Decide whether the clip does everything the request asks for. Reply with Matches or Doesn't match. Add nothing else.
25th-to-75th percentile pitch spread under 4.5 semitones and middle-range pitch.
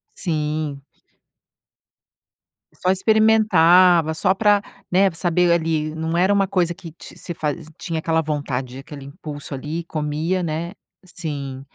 Matches